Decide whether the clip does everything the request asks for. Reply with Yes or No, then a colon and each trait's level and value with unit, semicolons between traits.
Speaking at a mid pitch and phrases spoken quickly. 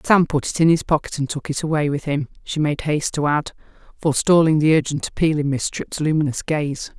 Yes: medium, 150 Hz; fast, 225 wpm